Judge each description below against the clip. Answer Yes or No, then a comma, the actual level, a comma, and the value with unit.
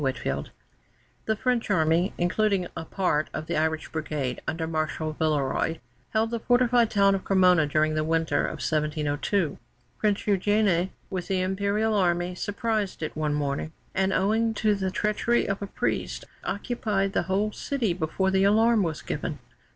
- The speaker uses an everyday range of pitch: Yes, average, 4.8 semitones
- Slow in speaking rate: No, average, 160 wpm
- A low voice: No, high, 190 Hz